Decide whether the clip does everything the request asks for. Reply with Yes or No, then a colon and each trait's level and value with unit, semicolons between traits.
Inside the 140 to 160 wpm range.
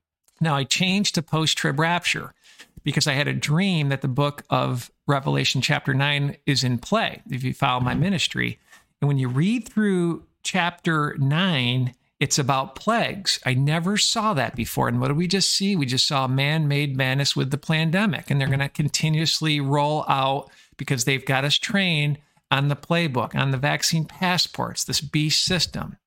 No: average, 175 wpm